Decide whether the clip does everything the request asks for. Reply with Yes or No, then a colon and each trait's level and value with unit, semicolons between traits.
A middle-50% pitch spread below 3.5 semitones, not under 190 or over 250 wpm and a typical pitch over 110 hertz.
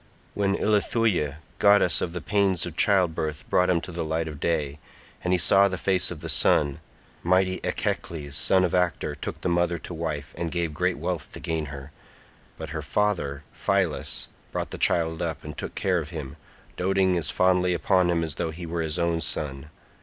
No: average, 2.9 semitones; average, 195 wpm; very low, 85 Hz